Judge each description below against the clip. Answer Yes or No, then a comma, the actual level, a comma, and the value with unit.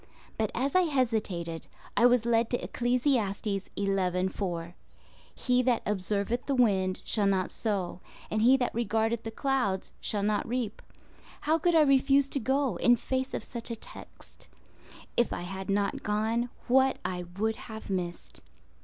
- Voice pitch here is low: No, high, 225 Hz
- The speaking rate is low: No, average, 155 wpm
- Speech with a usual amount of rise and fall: Yes, average, 4.2 semitones